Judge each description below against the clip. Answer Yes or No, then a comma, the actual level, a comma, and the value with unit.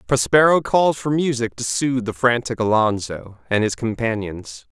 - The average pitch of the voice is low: Yes, low, 120 Hz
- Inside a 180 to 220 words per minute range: No, average, 150 wpm